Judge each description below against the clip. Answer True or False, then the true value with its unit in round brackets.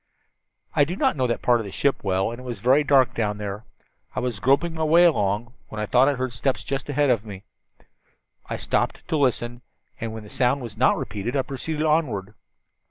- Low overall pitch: True (125 Hz)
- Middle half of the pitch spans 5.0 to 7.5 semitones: False (4.5 semitones)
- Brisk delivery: True (220 wpm)